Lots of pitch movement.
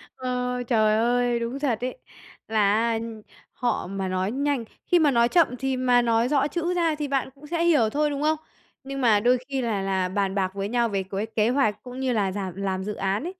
No: average, 4.9 semitones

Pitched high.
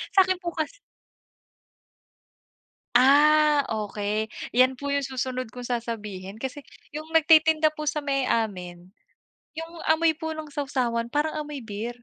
Yes: very high, 275 Hz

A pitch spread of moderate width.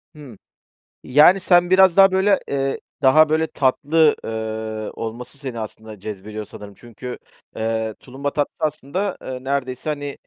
No: wide, 5.8 semitones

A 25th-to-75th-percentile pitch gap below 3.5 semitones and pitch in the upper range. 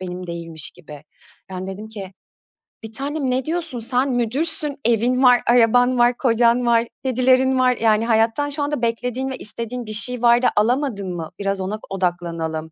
No: average, 4.4 semitones; high, 235 Hz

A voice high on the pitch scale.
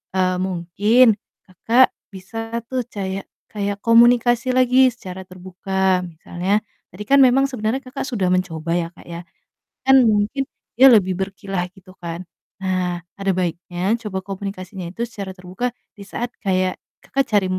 Yes: high, 195 Hz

